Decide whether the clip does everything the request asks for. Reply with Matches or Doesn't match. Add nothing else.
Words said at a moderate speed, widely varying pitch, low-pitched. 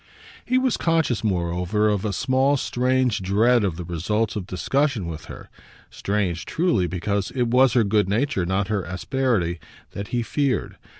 Matches